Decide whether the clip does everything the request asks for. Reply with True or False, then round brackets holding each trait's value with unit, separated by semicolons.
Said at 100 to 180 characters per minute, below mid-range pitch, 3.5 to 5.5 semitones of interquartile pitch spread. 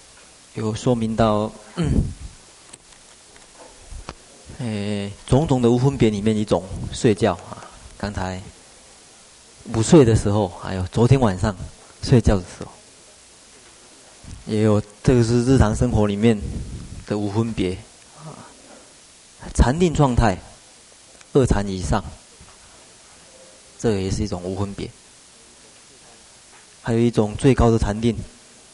False (160 characters per minute; 110 Hz; 2.5 semitones)